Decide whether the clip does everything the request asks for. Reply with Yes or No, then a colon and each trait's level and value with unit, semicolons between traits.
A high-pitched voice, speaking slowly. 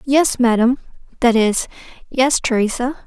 Yes: high, 245 Hz; slow, 100 wpm